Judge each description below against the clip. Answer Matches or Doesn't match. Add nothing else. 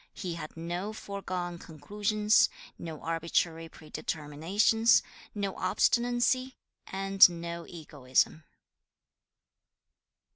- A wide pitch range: Doesn't match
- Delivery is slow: Matches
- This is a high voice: Doesn't match